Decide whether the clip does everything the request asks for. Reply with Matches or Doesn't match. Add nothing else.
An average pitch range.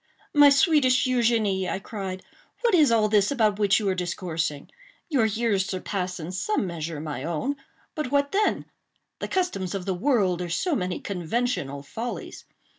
Doesn't match